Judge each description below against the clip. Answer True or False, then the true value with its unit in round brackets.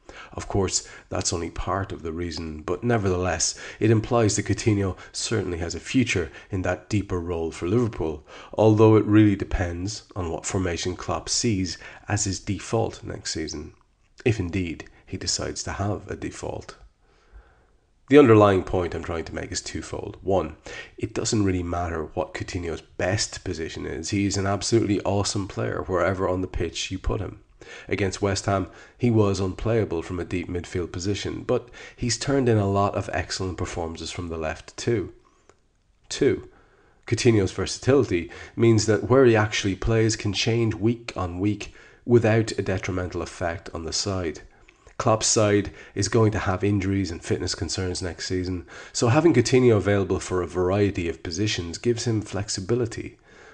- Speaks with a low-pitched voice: True (100 Hz)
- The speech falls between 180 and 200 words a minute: False (165 wpm)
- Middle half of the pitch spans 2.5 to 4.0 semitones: True (3.2 semitones)